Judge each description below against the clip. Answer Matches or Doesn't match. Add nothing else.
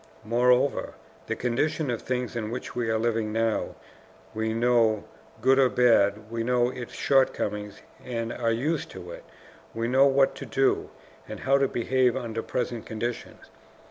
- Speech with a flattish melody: Matches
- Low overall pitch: Matches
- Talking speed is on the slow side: Doesn't match